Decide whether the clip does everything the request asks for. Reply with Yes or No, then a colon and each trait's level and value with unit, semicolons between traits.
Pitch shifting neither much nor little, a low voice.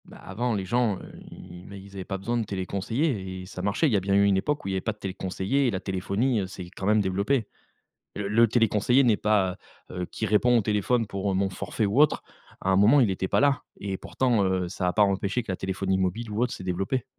Yes: average, 3.4 semitones; low, 100 Hz